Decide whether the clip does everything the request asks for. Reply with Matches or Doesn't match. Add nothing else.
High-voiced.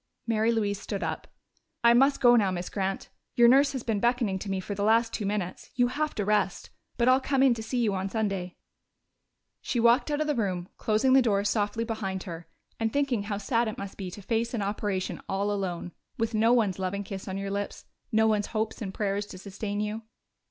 Matches